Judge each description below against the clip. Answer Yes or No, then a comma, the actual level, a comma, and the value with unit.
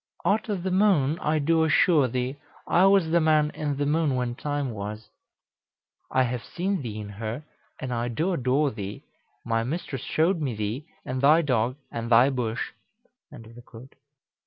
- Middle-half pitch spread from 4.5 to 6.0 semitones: Yes, average, 5.1 semitones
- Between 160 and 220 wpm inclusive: Yes, average, 175 wpm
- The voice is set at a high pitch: No, medium, 140 Hz